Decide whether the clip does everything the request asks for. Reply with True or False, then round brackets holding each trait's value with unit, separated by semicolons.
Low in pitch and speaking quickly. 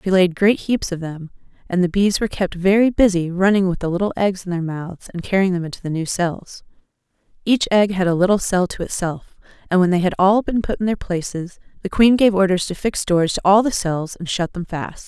False (185 Hz; 245 wpm)